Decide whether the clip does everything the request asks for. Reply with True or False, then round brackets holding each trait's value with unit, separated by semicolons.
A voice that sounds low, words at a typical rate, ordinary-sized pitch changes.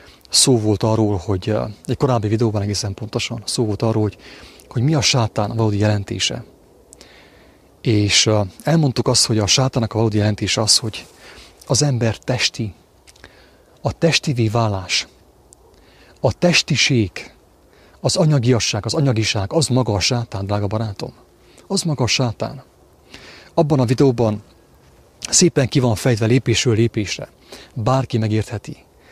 False (115 Hz; 130 wpm; 3.5 semitones)